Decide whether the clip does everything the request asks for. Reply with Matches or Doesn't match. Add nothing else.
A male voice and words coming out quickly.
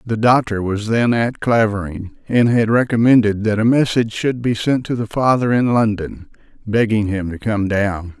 Doesn't match